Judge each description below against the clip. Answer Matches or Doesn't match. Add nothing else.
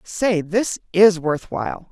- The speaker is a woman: Matches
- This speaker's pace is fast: Doesn't match